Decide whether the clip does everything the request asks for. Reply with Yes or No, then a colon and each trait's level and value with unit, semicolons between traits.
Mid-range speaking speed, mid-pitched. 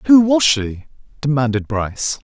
No: slow, 130 wpm; medium, 145 Hz